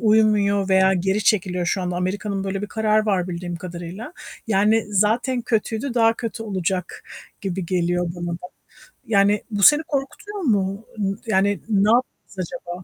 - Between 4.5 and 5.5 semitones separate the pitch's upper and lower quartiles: No, average, 3.1 semitones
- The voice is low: No, high, 200 Hz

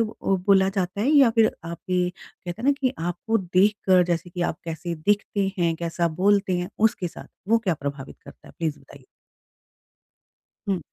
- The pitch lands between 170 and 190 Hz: Yes, medium, 185 Hz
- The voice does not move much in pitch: No, average, 3.1 semitones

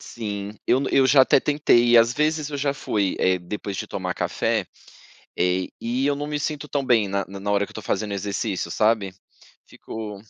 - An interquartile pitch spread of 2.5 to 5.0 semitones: No, wide, 5.6 semitones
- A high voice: No, low, 110 Hz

